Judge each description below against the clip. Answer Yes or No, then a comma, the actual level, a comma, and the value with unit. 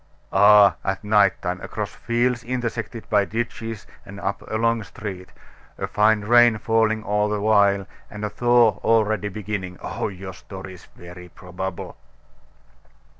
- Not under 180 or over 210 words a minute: No, average, 145 wpm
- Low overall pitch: Yes, low, 105 Hz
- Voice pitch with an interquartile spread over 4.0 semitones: No, average, 2.7 semitones